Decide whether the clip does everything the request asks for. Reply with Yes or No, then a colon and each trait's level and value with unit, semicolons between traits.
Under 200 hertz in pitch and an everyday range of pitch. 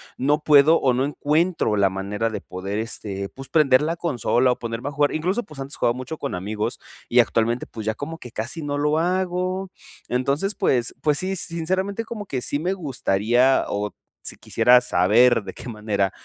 No: low, 135 Hz; wide, 6.2 semitones